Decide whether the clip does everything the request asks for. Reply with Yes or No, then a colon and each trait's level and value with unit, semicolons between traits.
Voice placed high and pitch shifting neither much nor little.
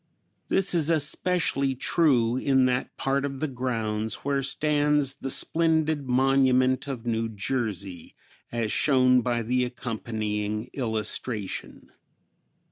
No: low, 130 Hz; average, 3.5 semitones